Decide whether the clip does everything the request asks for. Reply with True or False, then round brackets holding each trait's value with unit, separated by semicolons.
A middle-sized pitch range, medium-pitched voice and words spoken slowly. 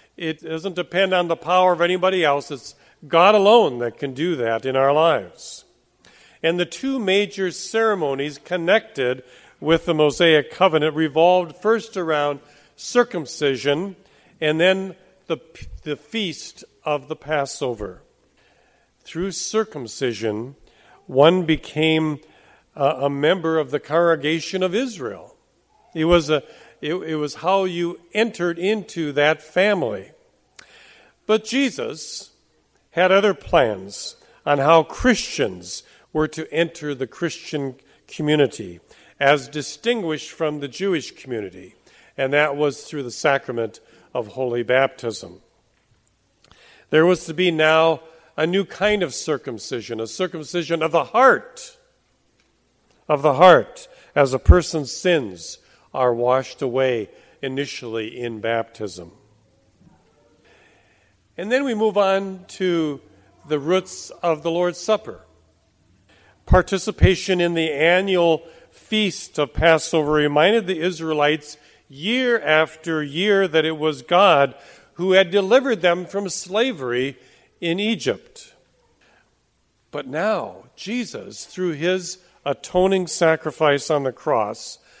True (4.7 semitones; 160 Hz; 120 wpm)